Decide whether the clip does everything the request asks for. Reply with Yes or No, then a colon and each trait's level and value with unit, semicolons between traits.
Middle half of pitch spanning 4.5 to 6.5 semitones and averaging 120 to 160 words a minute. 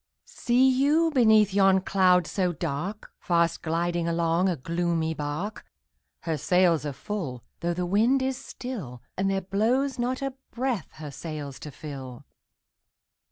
Yes: wide, 5.5 semitones; average, 145 wpm